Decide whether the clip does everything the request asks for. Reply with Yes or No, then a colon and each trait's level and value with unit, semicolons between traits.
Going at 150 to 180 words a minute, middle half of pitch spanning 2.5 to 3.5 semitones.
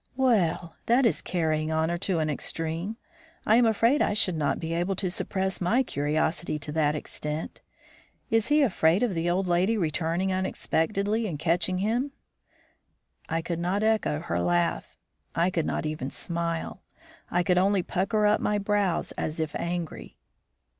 No: average, 160 wpm; average, 4.2 semitones